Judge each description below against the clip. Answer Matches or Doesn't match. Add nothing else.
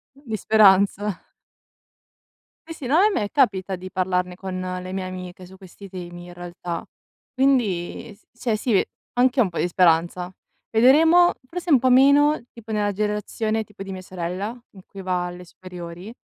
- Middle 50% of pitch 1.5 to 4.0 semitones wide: Doesn't match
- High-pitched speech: Matches